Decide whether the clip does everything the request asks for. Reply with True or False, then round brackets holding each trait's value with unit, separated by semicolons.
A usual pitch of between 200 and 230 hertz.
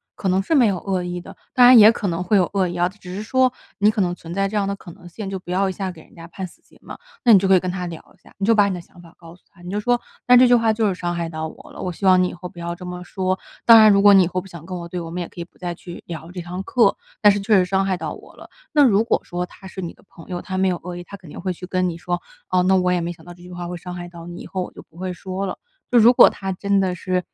False (185 Hz)